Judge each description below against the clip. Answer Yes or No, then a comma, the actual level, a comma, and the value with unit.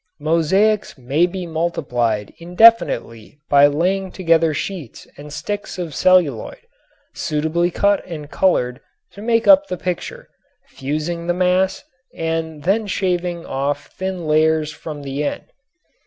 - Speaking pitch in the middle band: Yes, medium, 165 Hz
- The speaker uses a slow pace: Yes, slow, 125 wpm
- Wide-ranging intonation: No, average, 3.9 semitones